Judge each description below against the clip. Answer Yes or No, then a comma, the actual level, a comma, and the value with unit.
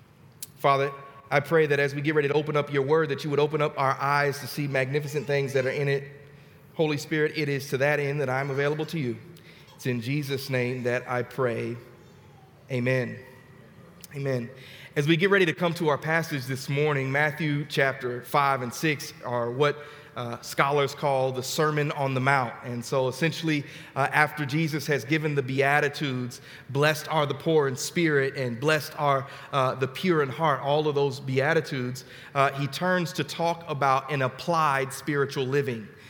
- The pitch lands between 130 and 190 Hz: Yes, medium, 140 Hz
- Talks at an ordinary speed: Yes, average, 190 wpm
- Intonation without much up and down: Yes, narrow, 2.3 semitones